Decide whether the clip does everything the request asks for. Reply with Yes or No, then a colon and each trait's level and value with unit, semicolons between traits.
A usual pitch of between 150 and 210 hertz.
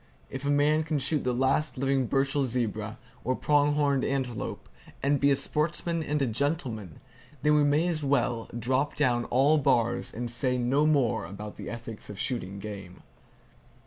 No: low, 135 Hz